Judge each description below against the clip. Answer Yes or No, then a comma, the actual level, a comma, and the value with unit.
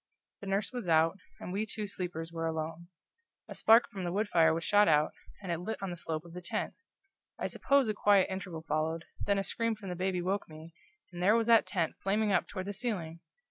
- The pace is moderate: No, fast, 230 wpm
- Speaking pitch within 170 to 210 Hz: Yes, medium, 185 Hz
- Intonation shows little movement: No, average, 3.8 semitones